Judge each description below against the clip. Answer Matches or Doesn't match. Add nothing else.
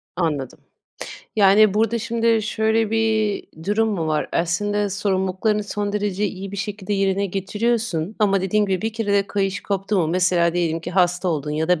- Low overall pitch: Doesn't match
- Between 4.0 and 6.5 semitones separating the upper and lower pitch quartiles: Doesn't match